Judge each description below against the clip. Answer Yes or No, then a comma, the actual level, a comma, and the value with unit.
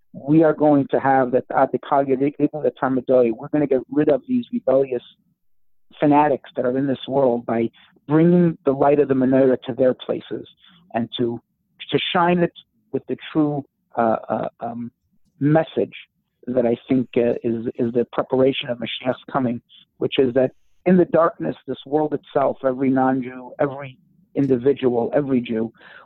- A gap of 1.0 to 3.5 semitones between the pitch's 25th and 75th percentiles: Yes, average, 2.9 semitones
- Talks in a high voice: No, low, 130 Hz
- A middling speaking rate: Yes, average, 170 wpm